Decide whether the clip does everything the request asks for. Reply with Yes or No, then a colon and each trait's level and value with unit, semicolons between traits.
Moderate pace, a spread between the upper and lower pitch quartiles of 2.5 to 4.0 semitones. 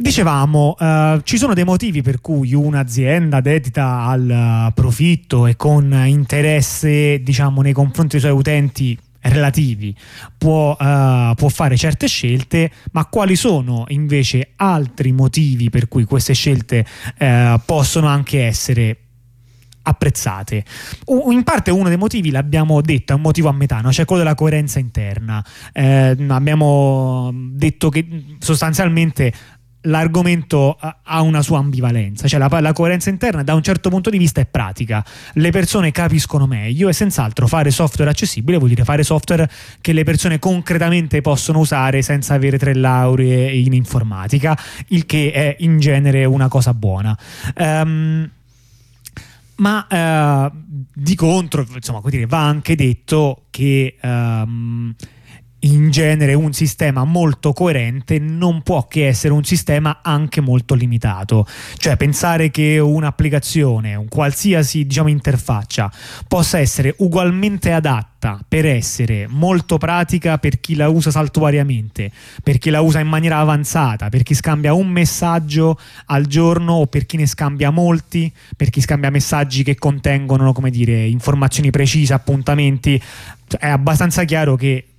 Yes: average, 140 wpm; average, 3.7 semitones